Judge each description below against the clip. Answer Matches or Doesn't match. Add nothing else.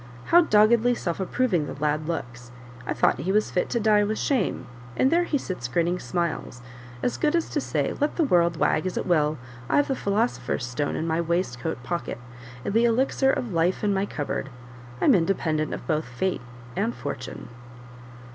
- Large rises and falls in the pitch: Matches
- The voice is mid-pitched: Matches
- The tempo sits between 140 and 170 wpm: Doesn't match